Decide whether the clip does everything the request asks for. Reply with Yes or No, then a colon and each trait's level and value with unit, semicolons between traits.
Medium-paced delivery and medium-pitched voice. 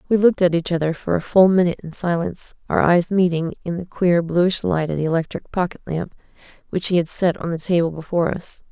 No: fast, 220 wpm; medium, 170 Hz